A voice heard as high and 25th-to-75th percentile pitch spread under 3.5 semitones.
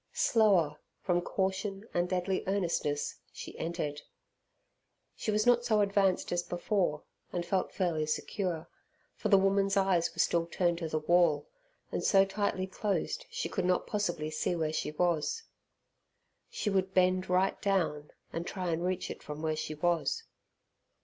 No: medium, 180 Hz; average, 2.7 semitones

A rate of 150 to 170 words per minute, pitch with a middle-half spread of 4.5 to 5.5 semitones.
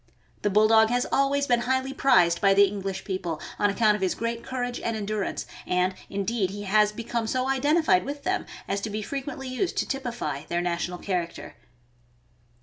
No: average, 185 wpm; average, 4.9 semitones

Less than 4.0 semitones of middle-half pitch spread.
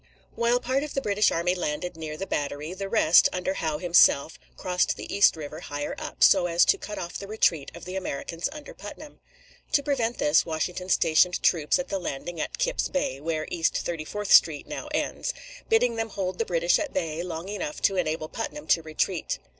No: average, 4.7 semitones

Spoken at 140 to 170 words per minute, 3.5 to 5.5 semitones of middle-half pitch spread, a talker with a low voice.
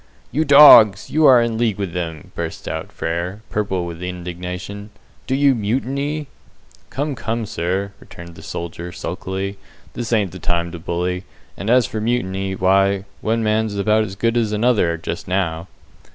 Yes: average, 165 wpm; average, 4.4 semitones; low, 100 Hz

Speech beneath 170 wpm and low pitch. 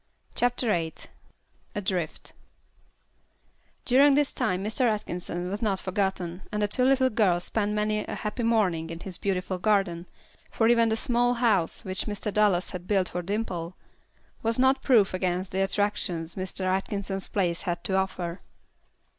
No: average, 155 wpm; high, 195 Hz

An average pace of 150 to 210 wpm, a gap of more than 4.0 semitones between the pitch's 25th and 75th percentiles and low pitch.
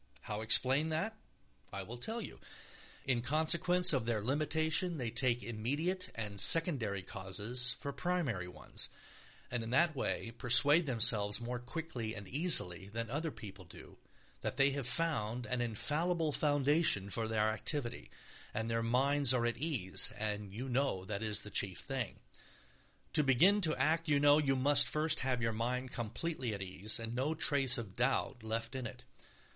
Yes: average, 165 wpm; average, 5.0 semitones; low, 125 Hz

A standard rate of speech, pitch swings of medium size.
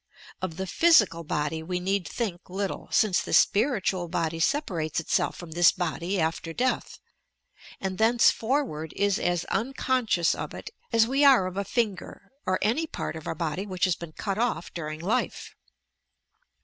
Yes: average, 160 wpm; average, 4.9 semitones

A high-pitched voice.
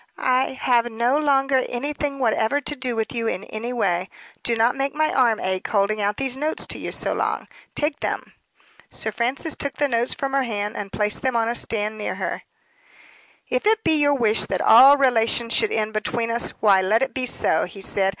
Yes: high, 240 Hz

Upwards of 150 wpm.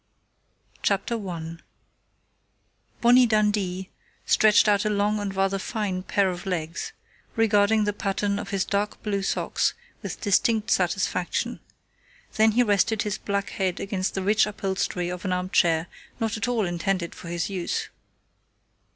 No: average, 145 wpm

